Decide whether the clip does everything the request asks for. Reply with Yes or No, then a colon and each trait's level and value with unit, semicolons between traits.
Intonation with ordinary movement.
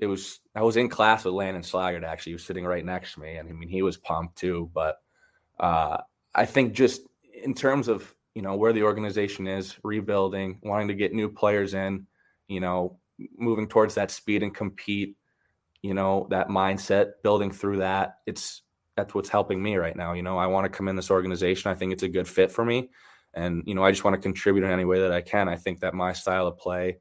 No: narrow, 2.2 semitones